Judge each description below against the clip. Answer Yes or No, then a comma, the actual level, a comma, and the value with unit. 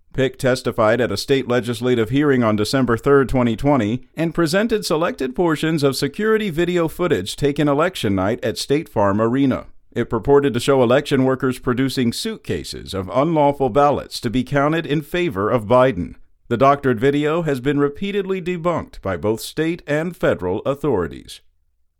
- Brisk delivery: No, average, 155 wpm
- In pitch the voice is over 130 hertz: Yes, medium, 140 Hz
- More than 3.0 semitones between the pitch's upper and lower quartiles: Yes, average, 4.2 semitones